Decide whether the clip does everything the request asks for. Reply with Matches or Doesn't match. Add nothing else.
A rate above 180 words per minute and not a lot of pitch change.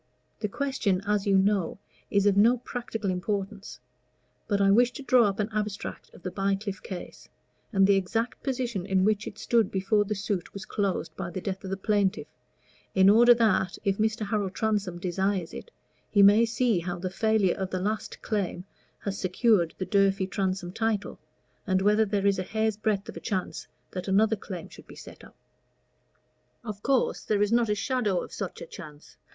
Matches